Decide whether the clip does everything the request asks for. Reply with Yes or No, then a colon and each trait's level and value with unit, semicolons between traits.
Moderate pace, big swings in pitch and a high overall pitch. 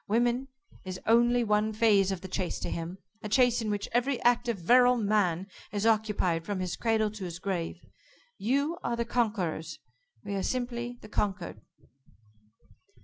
No: average, 160 wpm; average, 3.9 semitones; high, 215 Hz